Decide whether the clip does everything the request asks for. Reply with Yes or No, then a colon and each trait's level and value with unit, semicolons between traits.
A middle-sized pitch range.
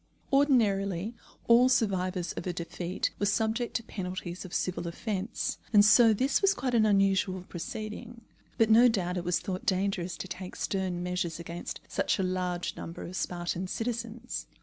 Yes: average, 3.9 semitones